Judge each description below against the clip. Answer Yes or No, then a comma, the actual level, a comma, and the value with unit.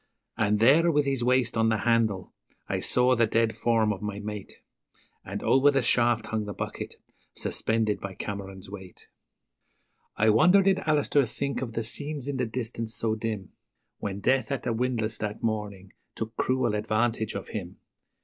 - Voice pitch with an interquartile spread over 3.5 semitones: No, average, 3.2 semitones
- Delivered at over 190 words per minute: No, average, 170 wpm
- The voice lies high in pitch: No, low, 115 Hz